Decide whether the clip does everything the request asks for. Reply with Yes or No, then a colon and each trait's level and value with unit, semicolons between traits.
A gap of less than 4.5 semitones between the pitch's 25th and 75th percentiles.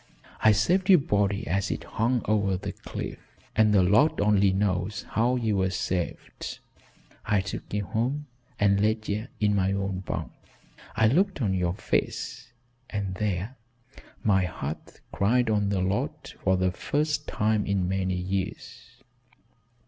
Yes: narrow, 2.5 semitones